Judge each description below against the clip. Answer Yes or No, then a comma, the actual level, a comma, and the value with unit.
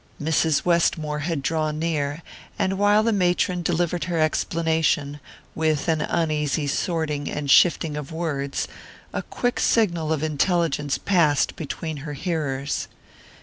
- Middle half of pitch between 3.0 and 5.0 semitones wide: No, narrow, 2.6 semitones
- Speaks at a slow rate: Yes, slow, 130 wpm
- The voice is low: No, medium, 160 Hz